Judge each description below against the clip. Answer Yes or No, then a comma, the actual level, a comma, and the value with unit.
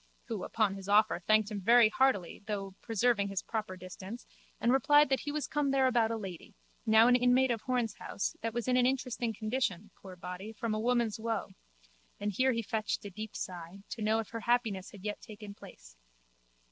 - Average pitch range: Yes, average, 3.3 semitones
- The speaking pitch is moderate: No, high, 220 Hz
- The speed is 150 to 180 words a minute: No, average, 200 wpm